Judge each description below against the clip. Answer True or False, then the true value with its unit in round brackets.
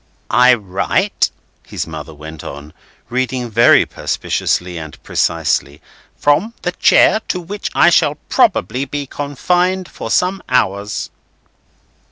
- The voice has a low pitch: True (125 Hz)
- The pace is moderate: False (120 wpm)